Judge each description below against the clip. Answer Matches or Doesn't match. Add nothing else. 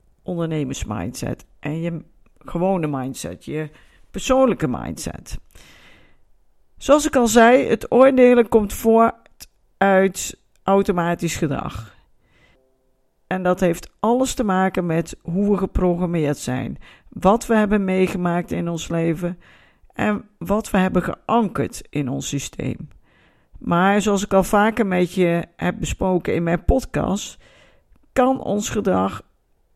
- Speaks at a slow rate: Matches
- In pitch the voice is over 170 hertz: Matches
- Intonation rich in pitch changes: Doesn't match